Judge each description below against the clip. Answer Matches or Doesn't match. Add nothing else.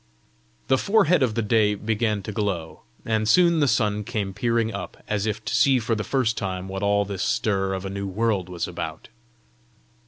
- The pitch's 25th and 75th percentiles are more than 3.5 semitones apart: Doesn't match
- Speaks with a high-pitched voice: Doesn't match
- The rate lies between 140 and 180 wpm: Doesn't match